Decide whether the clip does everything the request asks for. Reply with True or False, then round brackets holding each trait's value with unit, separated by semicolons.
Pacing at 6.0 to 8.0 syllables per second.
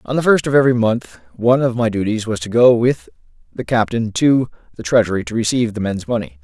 True (6.3 syllables/s)